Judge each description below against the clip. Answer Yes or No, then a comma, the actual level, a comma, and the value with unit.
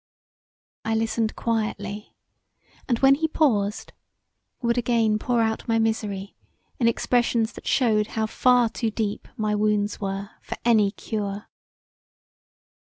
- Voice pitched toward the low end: No, high, 220 Hz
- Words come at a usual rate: No, slow, 125 wpm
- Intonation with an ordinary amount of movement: No, narrow, 2.0 semitones